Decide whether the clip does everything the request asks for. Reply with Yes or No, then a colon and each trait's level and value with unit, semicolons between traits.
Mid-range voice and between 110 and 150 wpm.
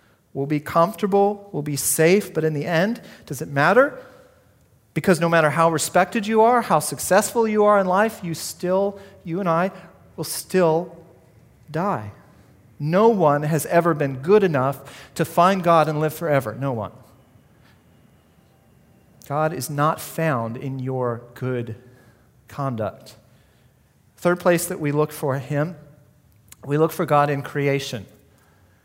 Yes: medium, 150 Hz; average, 145 wpm